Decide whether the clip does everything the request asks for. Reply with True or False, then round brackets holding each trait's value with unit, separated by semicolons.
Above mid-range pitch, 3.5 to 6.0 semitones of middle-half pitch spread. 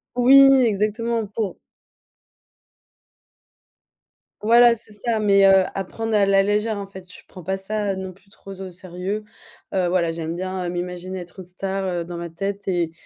False (195 Hz; 2.7 semitones)